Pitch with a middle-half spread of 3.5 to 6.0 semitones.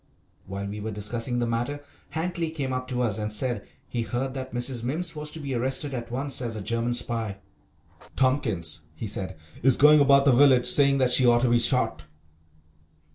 No: average, 3.1 semitones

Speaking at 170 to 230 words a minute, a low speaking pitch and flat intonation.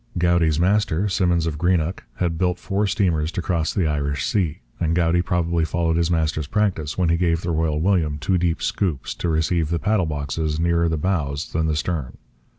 Yes: average, 195 wpm; very low, 85 Hz; narrow, 2.2 semitones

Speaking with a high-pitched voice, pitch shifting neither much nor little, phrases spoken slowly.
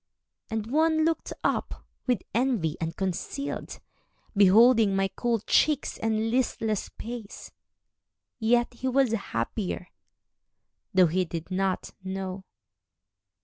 Yes: high, 220 Hz; average, 4.4 semitones; slow, 105 wpm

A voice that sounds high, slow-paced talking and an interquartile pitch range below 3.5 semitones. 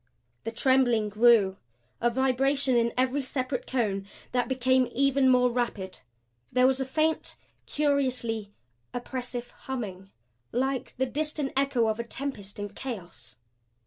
Yes: very high, 250 Hz; slow, 130 wpm; narrow, 2.6 semitones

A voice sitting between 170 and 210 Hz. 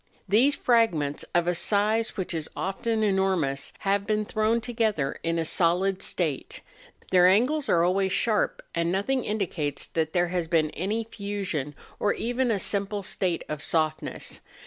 Yes: high, 190 Hz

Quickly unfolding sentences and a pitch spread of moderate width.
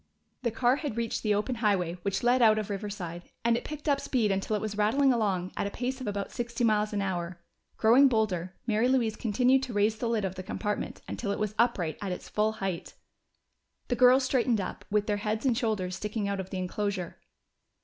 Yes: fast, 220 wpm; average, 3.3 semitones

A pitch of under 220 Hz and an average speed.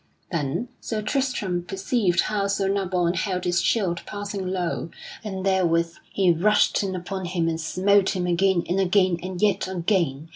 Yes: medium, 185 Hz; average, 160 wpm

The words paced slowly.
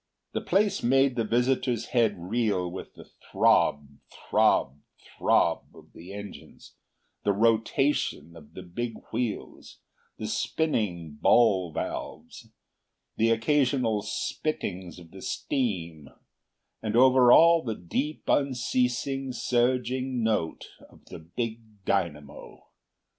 Yes: slow, 110 wpm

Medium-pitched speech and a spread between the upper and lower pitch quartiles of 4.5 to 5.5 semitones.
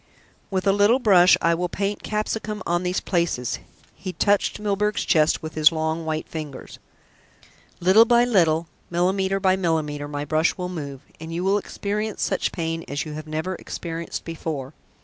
No: medium, 175 Hz; average, 3.8 semitones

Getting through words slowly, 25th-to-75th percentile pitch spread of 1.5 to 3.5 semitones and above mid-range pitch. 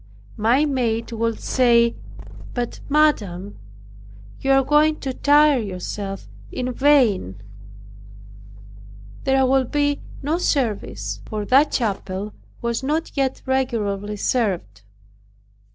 No: slow, 105 wpm; average, 4.9 semitones; high, 245 Hz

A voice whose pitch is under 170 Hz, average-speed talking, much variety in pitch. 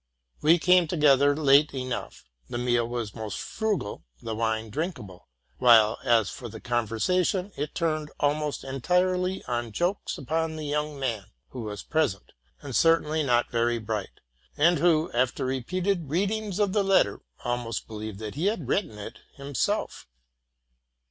Yes: medium, 140 Hz; average, 150 wpm; wide, 6.2 semitones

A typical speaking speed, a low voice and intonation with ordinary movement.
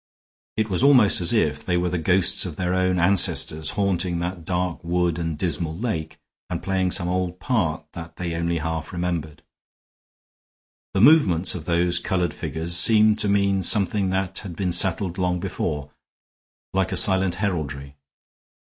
No: average, 160 wpm; very low, 90 Hz; narrow, 2.3 semitones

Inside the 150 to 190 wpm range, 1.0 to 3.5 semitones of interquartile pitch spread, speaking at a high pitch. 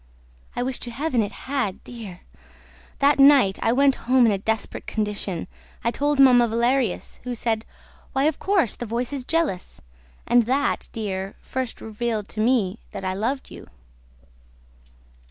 No: average, 155 wpm; average, 3.9 semitones; high, 240 Hz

